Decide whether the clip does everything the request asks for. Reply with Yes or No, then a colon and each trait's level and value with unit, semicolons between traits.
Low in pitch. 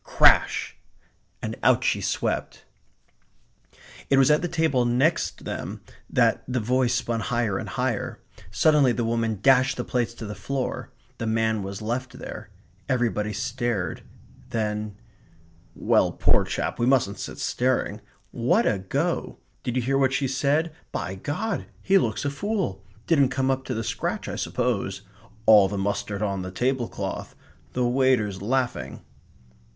Yes: low, 120 Hz